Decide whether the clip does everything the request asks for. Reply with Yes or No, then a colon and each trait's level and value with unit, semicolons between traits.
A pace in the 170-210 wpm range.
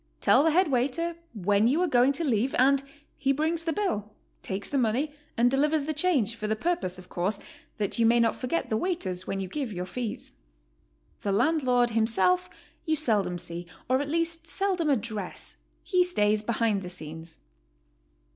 Yes: average, 180 wpm